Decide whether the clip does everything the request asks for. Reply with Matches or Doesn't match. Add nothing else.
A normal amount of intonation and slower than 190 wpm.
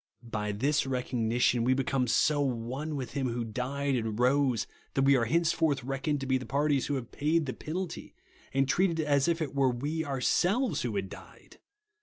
Doesn't match